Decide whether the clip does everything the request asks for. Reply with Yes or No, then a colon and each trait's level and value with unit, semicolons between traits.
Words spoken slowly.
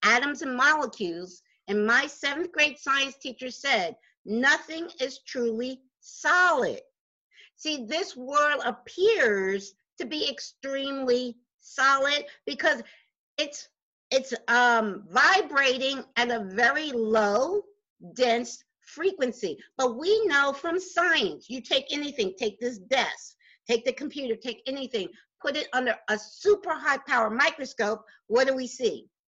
Yes: slow, 125 wpm